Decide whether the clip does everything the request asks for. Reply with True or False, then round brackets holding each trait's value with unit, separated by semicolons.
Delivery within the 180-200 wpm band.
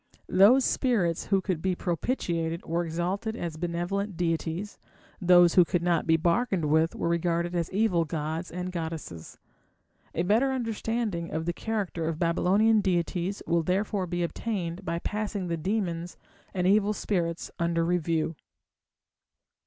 False (145 wpm)